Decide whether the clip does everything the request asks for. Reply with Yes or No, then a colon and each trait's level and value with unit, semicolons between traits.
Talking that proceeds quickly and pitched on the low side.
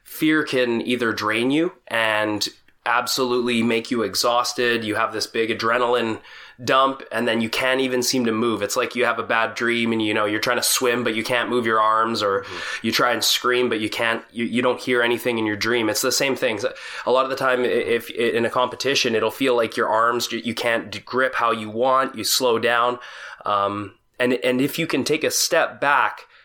Yes: fast, 225 wpm; low, 120 Hz